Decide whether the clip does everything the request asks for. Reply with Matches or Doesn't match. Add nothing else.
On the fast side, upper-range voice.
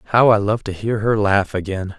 Doesn't match